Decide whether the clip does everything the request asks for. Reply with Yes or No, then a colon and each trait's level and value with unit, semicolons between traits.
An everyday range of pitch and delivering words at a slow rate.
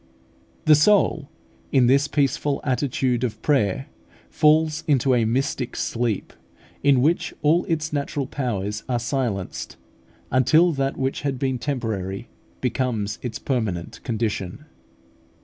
Yes: average, 3.7 semitones; slow, 120 wpm